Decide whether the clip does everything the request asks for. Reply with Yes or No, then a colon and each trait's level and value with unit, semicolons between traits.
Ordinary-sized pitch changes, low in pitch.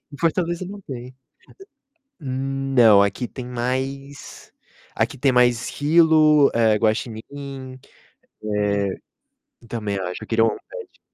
Yes: average, 4.1 semitones; low, 130 Hz